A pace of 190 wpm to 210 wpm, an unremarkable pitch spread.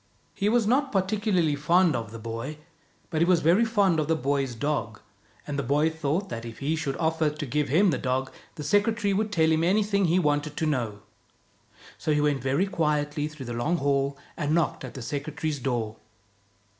Yes: average, 200 wpm; average, 4.3 semitones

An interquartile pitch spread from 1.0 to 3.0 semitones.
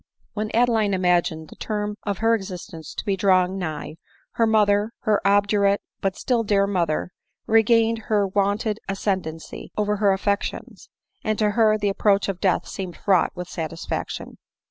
Yes: narrow, 2.5 semitones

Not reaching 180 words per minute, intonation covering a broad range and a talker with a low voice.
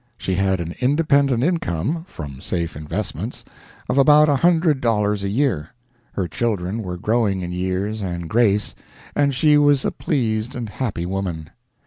Yes: average, 155 wpm; wide, 7.2 semitones; low, 110 Hz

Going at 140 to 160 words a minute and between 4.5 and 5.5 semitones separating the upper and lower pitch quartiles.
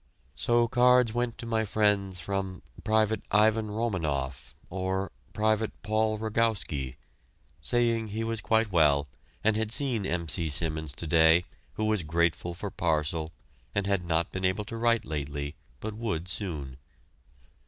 Yes: average, 145 wpm; average, 5.2 semitones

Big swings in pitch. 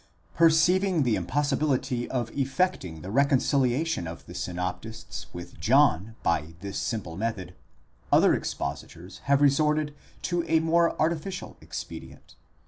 Yes: wide, 8.5 semitones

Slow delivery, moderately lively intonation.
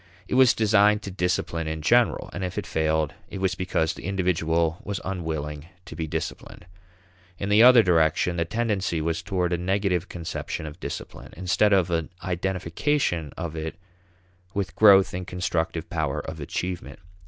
No: average, 165 wpm; average, 3.2 semitones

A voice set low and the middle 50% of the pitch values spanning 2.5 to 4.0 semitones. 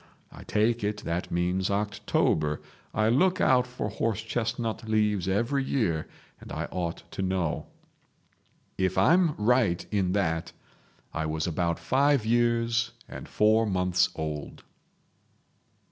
No: low, 105 Hz; average, 4.6 semitones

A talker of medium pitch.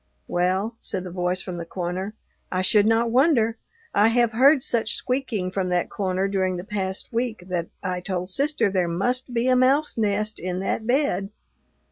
No: high, 200 Hz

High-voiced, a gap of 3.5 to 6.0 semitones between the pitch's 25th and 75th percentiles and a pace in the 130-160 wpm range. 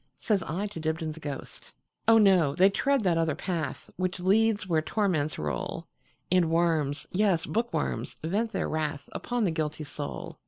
No: medium, 170 Hz; average, 4.4 semitones; slow, 135 wpm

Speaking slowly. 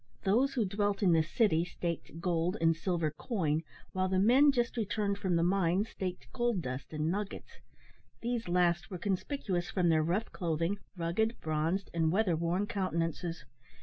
No: average, 165 wpm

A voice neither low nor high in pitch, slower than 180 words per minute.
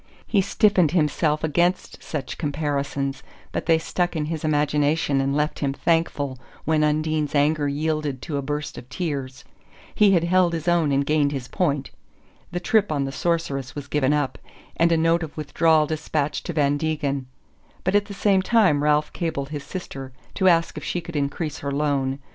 No: medium, 150 Hz; average, 185 wpm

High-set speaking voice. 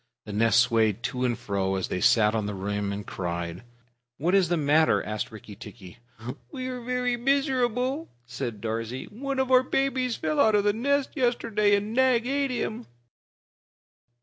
Yes: high, 195 Hz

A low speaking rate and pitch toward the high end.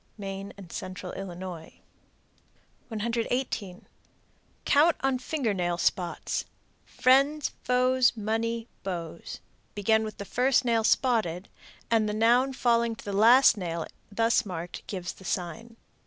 Yes: slow, 125 wpm; high, 220 Hz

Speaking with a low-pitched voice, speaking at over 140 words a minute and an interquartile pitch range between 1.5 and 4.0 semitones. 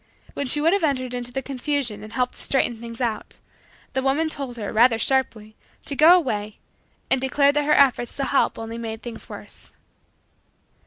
No: very high, 255 Hz; average, 190 wpm; average, 3.4 semitones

